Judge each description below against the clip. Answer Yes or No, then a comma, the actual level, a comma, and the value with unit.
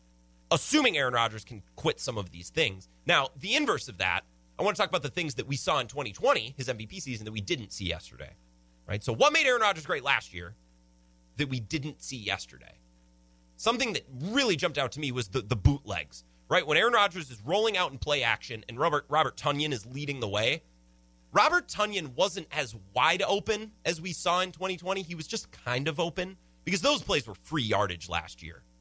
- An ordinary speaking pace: No, fast, 210 wpm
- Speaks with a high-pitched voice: No, low, 125 Hz